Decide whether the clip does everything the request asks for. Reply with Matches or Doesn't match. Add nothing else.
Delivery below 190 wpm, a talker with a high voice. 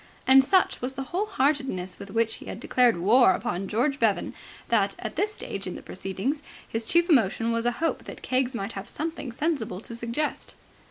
Doesn't match